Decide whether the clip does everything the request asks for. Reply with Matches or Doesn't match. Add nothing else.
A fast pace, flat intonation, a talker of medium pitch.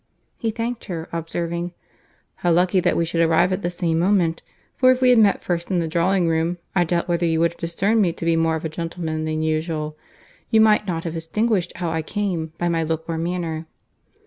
Matches